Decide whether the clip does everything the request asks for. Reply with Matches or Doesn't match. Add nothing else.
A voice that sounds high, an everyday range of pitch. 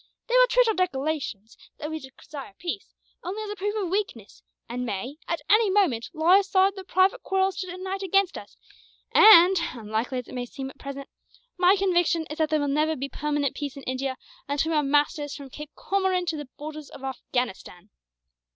Doesn't match